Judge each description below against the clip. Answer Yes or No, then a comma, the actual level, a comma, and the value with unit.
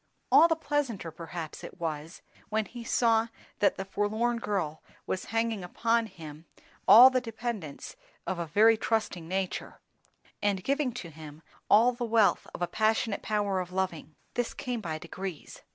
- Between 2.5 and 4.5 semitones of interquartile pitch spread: No, average, 5.2 semitones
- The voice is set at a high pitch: Yes, high, 205 Hz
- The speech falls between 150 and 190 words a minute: Yes, average, 160 wpm